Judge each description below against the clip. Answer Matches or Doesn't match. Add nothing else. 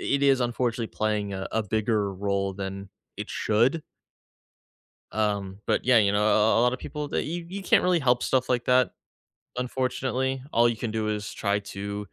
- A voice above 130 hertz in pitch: Doesn't match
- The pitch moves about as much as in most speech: Matches